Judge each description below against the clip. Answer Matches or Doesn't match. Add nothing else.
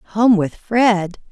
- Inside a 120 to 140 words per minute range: Matches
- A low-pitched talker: Doesn't match